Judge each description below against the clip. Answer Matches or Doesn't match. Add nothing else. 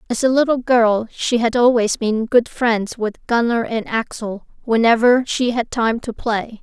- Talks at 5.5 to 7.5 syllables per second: Doesn't match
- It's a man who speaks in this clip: Doesn't match